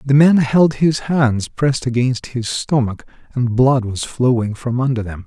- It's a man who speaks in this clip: Yes, male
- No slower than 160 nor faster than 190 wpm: Yes, average, 180 wpm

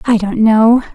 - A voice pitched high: Yes, high, 220 Hz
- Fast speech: No, average, 190 wpm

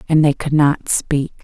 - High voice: No, medium, 145 Hz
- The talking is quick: Yes, fast, 210 wpm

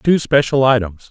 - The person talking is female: No, male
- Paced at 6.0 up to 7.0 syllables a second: No, 4.7 syllables/s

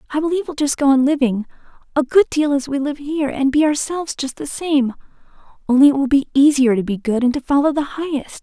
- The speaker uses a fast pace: Yes, fast, 215 wpm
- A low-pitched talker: No, very high, 280 Hz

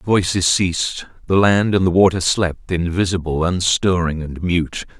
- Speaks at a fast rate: No, average, 155 wpm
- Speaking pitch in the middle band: No, very low, 90 Hz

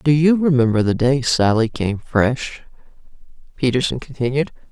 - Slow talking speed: Yes, slow, 125 wpm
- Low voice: Yes, low, 130 Hz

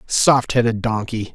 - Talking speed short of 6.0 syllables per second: Yes, 4.1 syllables/s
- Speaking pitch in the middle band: No, low, 115 Hz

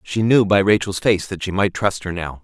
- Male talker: Yes, male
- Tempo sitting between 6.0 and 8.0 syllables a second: No, 5.2 syllables/s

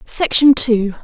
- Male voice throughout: No, female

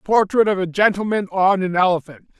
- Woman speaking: No, male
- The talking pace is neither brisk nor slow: Yes, average, 175 wpm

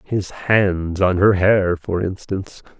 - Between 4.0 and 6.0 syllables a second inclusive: No, 3.5 syllables/s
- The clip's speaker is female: No, male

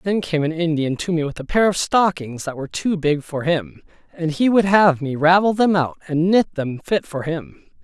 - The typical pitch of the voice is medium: Yes, medium, 165 Hz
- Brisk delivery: Yes, fast, 235 wpm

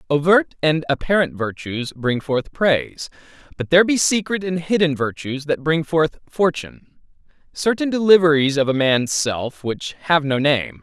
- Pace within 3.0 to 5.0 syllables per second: Yes, 4.6 syllables/s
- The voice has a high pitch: No, medium, 155 Hz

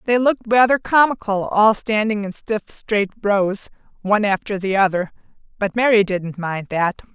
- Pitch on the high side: Yes, high, 205 Hz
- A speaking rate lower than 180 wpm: Yes, average, 170 wpm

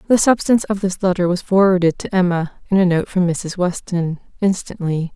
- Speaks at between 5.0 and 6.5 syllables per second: Yes, 5.4 syllables/s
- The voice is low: No, medium, 185 Hz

